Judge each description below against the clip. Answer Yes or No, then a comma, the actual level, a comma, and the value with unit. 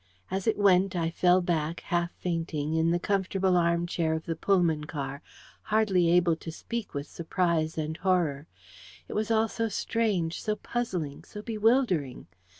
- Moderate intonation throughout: Yes, average, 3.6 semitones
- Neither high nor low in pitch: Yes, medium, 175 Hz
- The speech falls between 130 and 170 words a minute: Yes, average, 155 wpm